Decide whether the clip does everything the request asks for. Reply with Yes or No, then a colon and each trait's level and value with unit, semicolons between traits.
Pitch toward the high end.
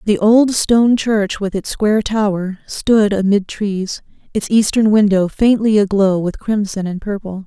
Yes: high, 205 Hz